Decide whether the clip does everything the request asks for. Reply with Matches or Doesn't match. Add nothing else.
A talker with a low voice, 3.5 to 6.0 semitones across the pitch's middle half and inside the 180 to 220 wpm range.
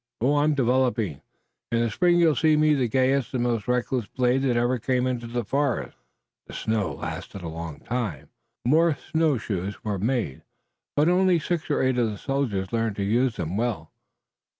Matches